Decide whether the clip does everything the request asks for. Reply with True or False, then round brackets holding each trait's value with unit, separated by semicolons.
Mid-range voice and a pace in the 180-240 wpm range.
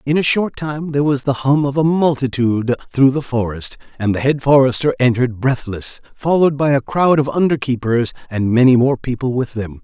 False (130 Hz; 200 wpm)